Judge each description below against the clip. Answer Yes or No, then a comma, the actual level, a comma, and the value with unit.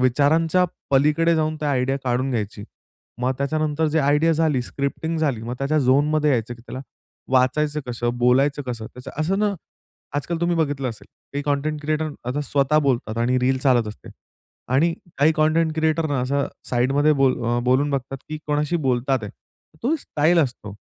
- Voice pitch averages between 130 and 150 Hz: Yes, medium, 140 Hz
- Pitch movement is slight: No, average, 3.4 semitones